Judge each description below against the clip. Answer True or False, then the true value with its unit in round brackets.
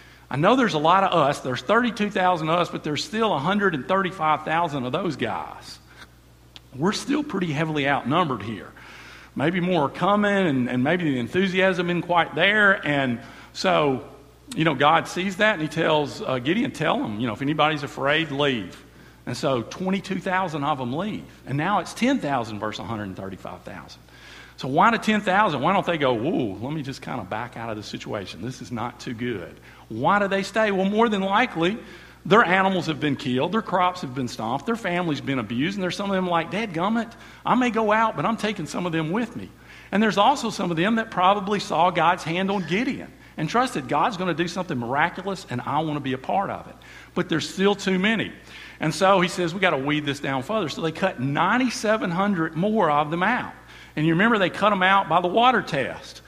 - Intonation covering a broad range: True (6.1 semitones)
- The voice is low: False (175 Hz)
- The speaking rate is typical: False (215 wpm)